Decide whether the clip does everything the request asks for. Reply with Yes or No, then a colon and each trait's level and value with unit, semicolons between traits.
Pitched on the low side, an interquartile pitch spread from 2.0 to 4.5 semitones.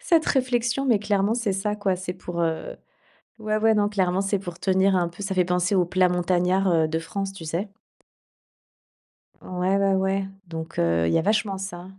No: high, 190 Hz; narrow, 2.5 semitones